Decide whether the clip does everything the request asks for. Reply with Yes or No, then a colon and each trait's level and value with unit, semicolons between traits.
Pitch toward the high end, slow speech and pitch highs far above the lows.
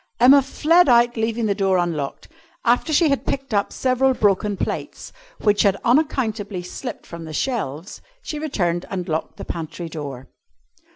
No: high, 210 Hz; average, 160 wpm; wide, 6.7 semitones